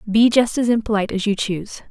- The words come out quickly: Yes, fast, 220 wpm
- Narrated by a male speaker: No, female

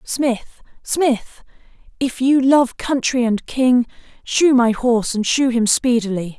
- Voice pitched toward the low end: No, high, 245 Hz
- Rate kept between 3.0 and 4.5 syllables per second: Yes, 3.8 syllables/s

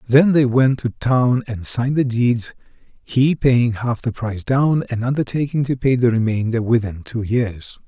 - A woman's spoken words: No, male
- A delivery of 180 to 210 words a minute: Yes, average, 185 wpm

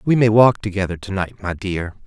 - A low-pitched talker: Yes, low, 100 Hz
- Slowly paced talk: No, fast, 205 wpm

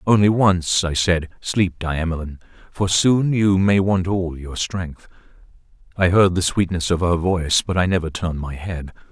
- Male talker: Yes, male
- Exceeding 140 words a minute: Yes, average, 180 wpm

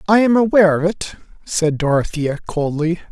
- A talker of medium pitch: Yes, medium, 175 Hz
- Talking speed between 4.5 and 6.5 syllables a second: Yes, 5.2 syllables/s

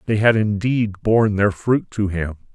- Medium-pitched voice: No, low, 105 Hz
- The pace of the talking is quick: No, average, 190 wpm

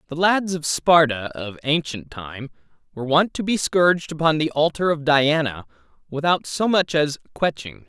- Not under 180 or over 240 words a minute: No, average, 170 wpm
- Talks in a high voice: No, medium, 150 Hz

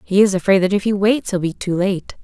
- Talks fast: Yes, fast, 295 wpm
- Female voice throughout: Yes, female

